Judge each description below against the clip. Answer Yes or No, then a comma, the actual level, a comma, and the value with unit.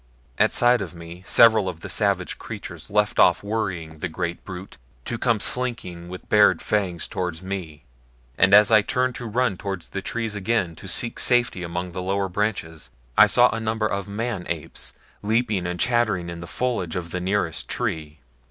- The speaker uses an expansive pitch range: No, average, 4.2 semitones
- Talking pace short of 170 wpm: No, average, 190 wpm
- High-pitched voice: No, very low, 95 Hz